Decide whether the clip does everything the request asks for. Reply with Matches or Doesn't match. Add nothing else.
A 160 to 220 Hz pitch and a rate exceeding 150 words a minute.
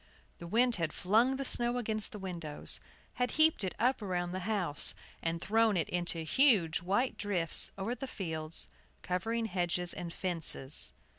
Matches